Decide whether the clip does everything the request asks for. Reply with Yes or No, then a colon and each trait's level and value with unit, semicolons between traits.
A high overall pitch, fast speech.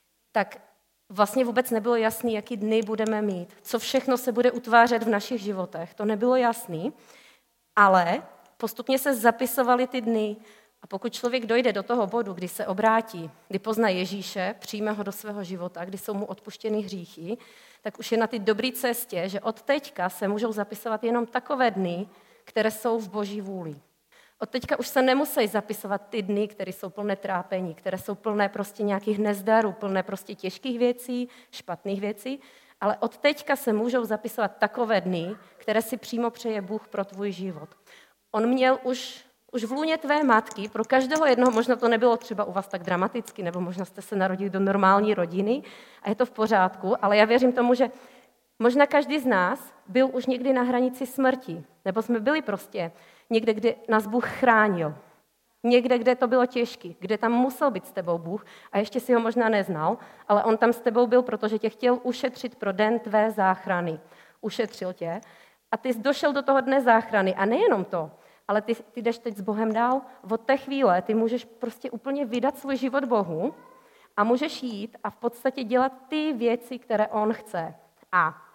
Yes: high, 225 Hz; fast, 185 wpm